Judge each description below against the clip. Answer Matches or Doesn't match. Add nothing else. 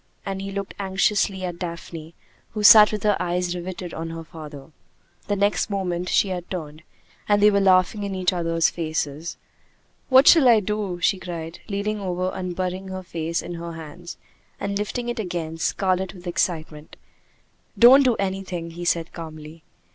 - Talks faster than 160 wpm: Matches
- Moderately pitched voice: Matches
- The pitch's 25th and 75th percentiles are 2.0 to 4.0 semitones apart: Matches